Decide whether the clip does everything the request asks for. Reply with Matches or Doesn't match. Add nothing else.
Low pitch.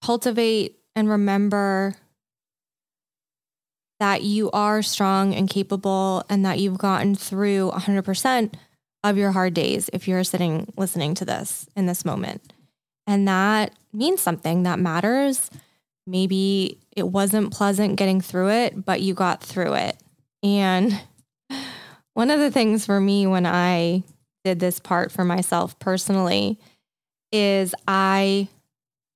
Doesn't match